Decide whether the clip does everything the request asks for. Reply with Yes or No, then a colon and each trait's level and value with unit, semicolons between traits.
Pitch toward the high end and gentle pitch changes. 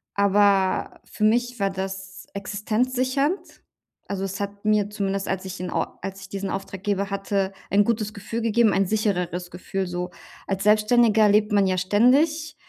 Yes: high, 200 Hz; narrow, 2.0 semitones